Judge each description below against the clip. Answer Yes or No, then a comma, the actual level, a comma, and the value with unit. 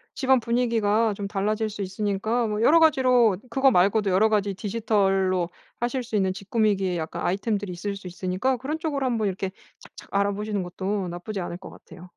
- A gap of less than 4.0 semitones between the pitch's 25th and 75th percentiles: Yes, average, 3.3 semitones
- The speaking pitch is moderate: No, high, 205 Hz